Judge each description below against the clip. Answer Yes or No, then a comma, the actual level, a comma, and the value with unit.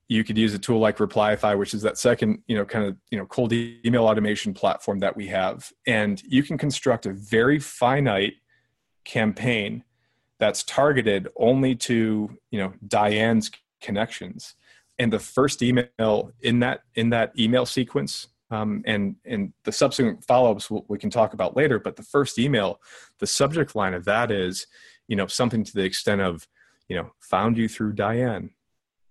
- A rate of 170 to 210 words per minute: Yes, average, 175 wpm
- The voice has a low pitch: Yes, low, 110 Hz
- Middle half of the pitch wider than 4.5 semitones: No, average, 2.7 semitones